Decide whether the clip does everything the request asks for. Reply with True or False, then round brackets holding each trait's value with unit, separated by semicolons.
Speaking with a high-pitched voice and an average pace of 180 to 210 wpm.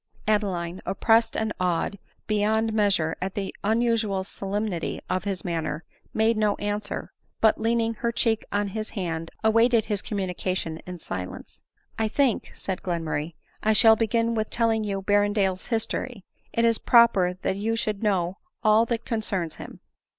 False (205 Hz; 160 wpm)